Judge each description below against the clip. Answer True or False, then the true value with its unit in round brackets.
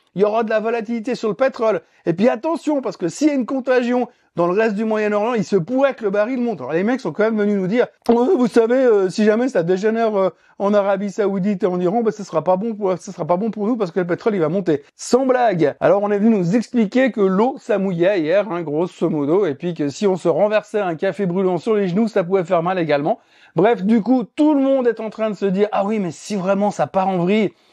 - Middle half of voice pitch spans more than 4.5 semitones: False (3.7 semitones)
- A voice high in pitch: True (210 Hz)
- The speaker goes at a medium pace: False (275 wpm)